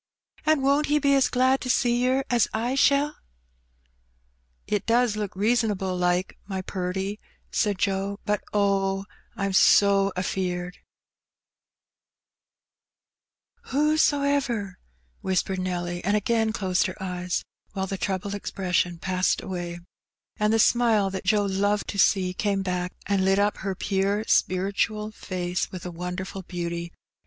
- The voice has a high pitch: Yes, high, 195 Hz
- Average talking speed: Yes, average, 145 wpm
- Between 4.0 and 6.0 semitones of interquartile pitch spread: No, average, 3.0 semitones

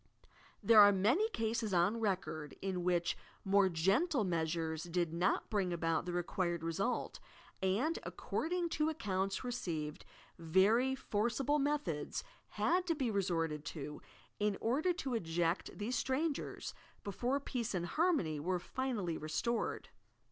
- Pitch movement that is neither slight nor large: No, wide, 6.7 semitones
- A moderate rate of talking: No, slow, 130 wpm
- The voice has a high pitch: Yes, high, 195 Hz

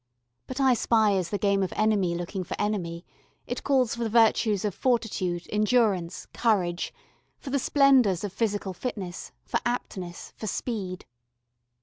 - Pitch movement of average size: Yes, average, 4.4 semitones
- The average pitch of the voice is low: No, high, 210 Hz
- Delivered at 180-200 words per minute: No, average, 150 wpm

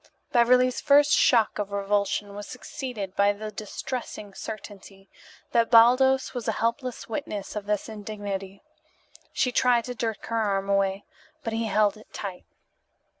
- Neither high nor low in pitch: No, high, 215 Hz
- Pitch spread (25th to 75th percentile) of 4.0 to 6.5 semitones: No, average, 3.3 semitones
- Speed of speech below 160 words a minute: Yes, average, 145 wpm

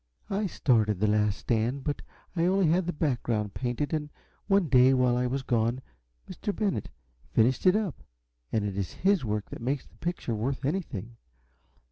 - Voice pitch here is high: No, low, 130 Hz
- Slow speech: No, average, 175 wpm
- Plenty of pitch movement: Yes, wide, 6.9 semitones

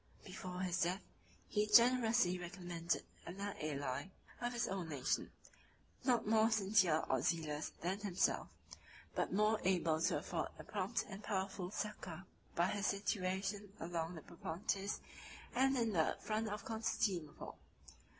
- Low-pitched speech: No, high, 190 Hz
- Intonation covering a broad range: No, average, 3.7 semitones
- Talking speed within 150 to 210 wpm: No, average, 140 wpm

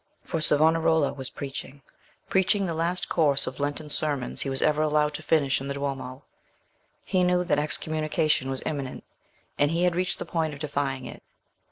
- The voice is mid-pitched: Yes, medium, 150 Hz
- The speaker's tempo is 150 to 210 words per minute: Yes, average, 175 wpm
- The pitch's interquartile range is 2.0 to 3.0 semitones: Yes, average, 2.7 semitones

